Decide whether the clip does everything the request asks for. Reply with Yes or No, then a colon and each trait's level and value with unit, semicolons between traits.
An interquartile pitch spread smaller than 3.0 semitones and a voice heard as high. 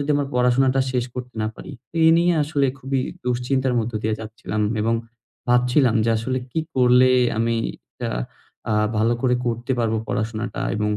No: narrow, 2.5 semitones; low, 125 Hz